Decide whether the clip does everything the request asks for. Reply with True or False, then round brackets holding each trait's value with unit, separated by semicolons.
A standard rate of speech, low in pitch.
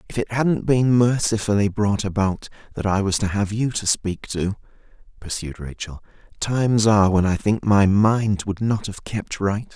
True (185 wpm; 105 Hz)